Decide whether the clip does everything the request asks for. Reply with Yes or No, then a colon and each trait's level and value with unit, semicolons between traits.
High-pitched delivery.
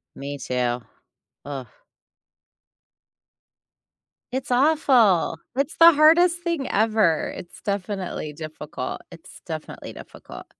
Yes: high, 205 Hz